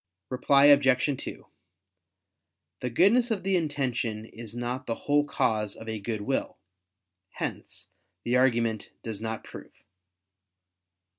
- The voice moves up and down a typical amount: Yes, average, 4.2 semitones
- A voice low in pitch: Yes, low, 125 Hz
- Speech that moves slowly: Yes, slow, 125 wpm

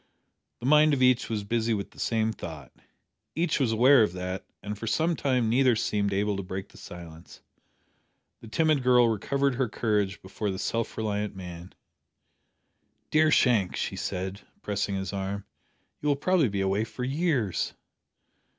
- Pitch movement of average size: Yes, average, 4.7 semitones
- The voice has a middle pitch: No, low, 110 Hz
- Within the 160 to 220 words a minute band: Yes, average, 165 wpm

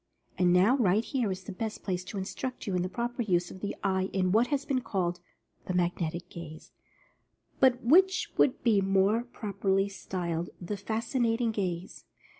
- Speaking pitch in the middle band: No, high, 195 Hz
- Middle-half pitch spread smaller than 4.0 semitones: No, average, 4.3 semitones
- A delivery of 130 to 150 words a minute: No, average, 180 wpm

